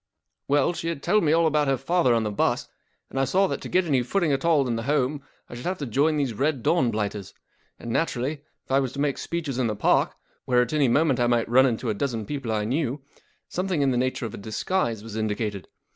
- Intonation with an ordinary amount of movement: Yes, average, 4.6 semitones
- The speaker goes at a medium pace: No, fast, 260 wpm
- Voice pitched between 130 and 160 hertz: Yes, low, 135 Hz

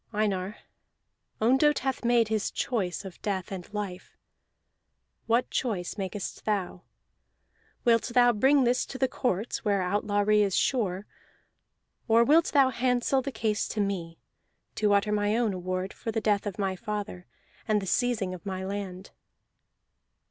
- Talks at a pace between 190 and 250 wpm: No, average, 150 wpm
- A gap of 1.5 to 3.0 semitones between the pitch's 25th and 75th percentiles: No, average, 3.7 semitones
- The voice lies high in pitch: Yes, high, 210 Hz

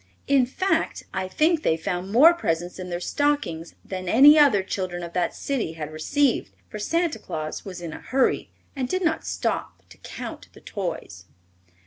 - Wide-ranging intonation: Yes, wide, 8.7 semitones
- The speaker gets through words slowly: No, average, 175 wpm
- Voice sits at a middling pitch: No, high, 200 Hz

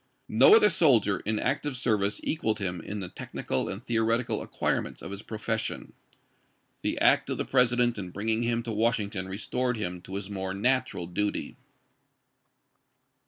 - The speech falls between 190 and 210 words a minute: No, average, 155 wpm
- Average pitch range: Yes, average, 3.8 semitones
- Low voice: Yes, low, 110 Hz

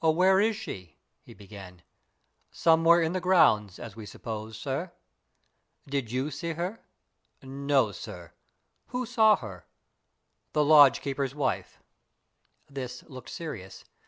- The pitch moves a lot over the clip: Yes, wide, 7.5 semitones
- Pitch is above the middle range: No, medium, 140 Hz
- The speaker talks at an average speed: No, slow, 125 wpm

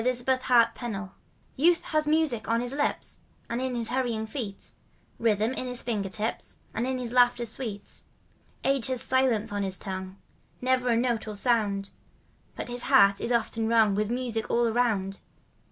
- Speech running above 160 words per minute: Yes, average, 185 wpm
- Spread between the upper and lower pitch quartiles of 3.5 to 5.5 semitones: No, average, 2.9 semitones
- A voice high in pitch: Yes, high, 235 Hz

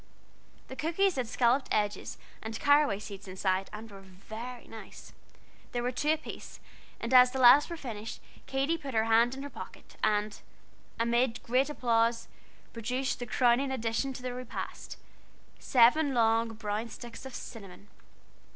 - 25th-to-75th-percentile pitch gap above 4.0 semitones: No, average, 3.1 semitones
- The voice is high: Yes, high, 240 Hz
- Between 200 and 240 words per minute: No, average, 150 wpm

